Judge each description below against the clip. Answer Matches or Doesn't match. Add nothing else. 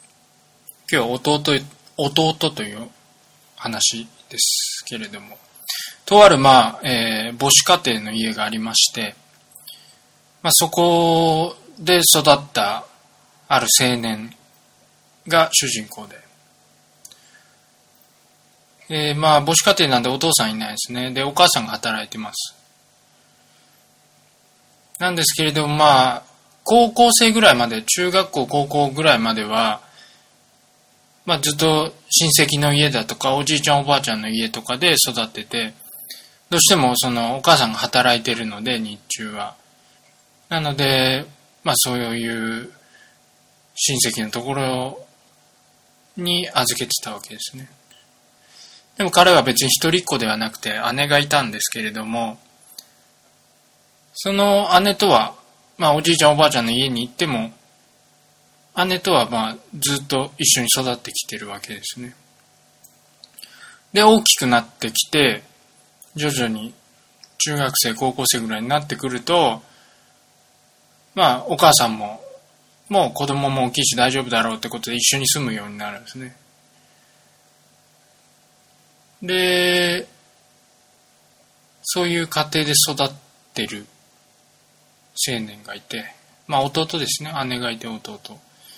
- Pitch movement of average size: Matches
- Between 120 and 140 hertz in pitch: Matches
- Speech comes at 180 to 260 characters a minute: Matches